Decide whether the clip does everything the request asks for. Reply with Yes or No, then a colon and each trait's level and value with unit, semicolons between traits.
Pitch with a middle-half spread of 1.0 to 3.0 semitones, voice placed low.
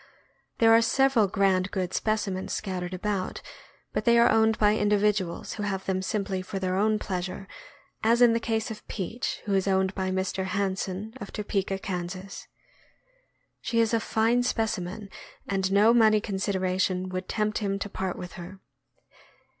No: narrow, 2.6 semitones; high, 200 Hz